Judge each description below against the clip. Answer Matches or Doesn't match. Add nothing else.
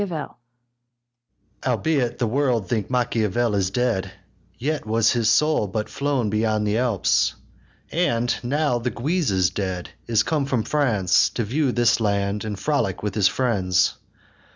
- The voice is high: Doesn't match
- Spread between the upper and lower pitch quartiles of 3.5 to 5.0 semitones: Matches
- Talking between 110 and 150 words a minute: Matches